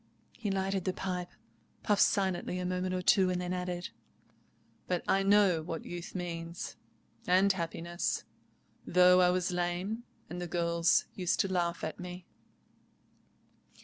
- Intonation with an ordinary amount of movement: No, narrow, 1.2 semitones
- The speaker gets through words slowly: No, average, 145 wpm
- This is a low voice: No, medium, 180 Hz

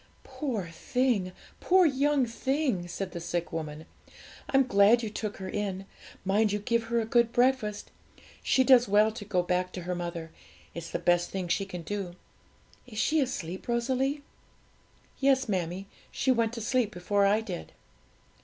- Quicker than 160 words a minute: Yes, average, 170 wpm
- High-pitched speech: Yes, high, 210 Hz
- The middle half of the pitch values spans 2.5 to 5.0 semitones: No, wide, 5.5 semitones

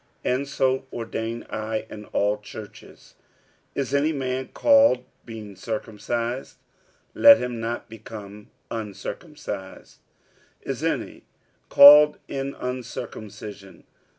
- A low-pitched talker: Yes, low, 115 Hz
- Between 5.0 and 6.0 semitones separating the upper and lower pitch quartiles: No, average, 3.8 semitones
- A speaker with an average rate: No, slow, 100 wpm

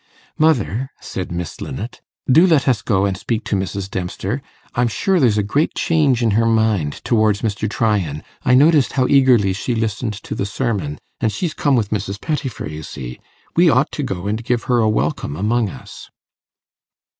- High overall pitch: No, low, 110 Hz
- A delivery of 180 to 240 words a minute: Yes, average, 185 wpm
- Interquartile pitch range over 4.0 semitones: Yes, average, 4.8 semitones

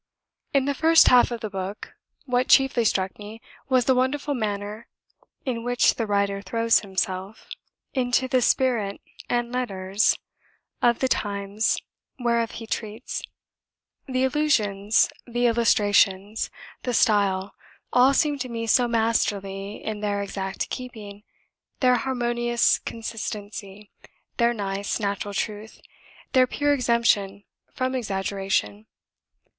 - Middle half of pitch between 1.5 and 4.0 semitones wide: Yes, average, 3.6 semitones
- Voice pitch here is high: Yes, high, 225 Hz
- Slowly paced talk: Yes, slow, 120 wpm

